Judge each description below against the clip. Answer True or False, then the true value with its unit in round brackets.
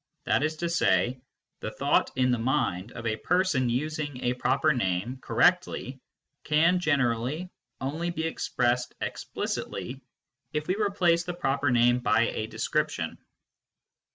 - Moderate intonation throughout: True (5.0 semitones)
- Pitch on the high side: False (135 Hz)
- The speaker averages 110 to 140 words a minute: True (135 wpm)